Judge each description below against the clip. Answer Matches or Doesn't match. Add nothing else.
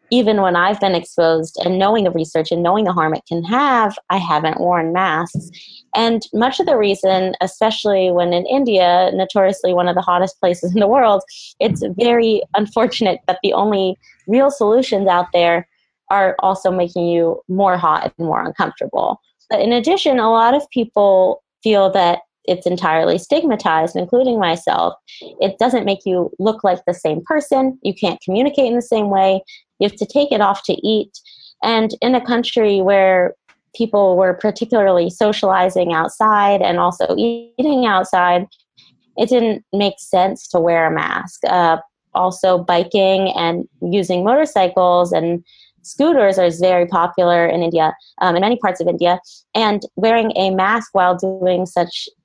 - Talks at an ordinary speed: Matches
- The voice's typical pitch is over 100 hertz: Matches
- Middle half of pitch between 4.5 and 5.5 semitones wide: Doesn't match